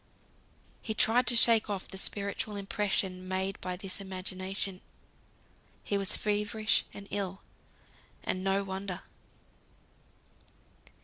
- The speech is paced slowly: Yes, slow, 110 wpm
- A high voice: Yes, high, 195 Hz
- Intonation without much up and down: Yes, narrow, 1.7 semitones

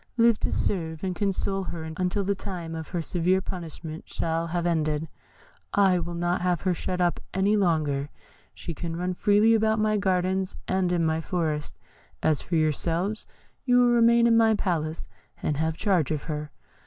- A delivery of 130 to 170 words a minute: No, average, 180 wpm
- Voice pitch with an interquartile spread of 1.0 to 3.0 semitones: No, average, 3.5 semitones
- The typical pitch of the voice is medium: Yes, medium, 175 Hz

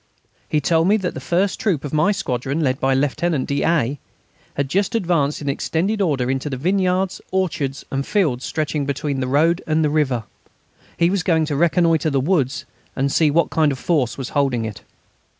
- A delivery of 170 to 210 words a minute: Yes, average, 190 wpm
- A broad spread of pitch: No, average, 4.1 semitones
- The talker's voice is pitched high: No, medium, 150 Hz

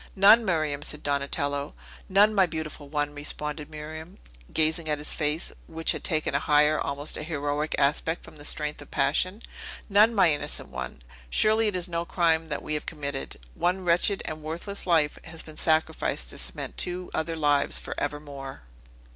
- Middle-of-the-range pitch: Yes, medium, 155 Hz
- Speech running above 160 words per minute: Yes, average, 175 wpm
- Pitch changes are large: No, average, 2.8 semitones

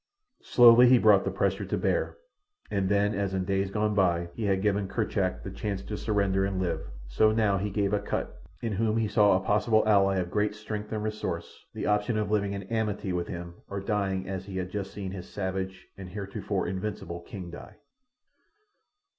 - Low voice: Yes, low, 100 Hz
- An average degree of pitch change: No, narrow, 1.9 semitones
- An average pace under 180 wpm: No, average, 195 wpm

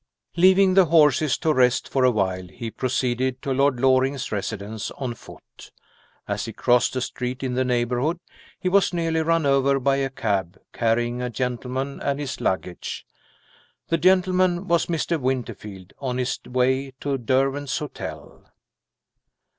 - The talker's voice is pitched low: Yes, low, 130 Hz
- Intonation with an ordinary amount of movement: Yes, average, 3.4 semitones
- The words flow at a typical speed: Yes, average, 150 wpm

